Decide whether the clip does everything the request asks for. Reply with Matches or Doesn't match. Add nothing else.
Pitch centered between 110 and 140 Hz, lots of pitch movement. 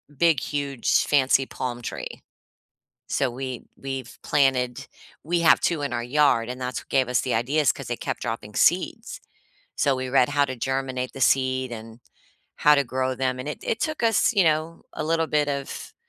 Doesn't match